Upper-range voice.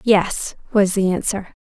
Yes: high, 195 Hz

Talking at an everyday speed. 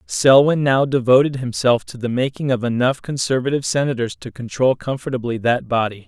Yes: average, 160 wpm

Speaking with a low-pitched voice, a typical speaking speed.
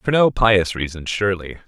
Yes: low, 100 Hz; average, 180 wpm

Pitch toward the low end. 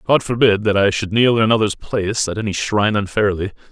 Yes: low, 105 Hz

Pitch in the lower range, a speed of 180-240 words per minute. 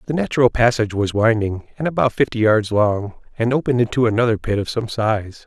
Yes: low, 115 Hz; average, 200 wpm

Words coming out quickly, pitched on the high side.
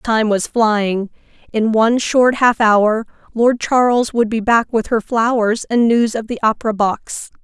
No: average, 180 wpm; high, 225 Hz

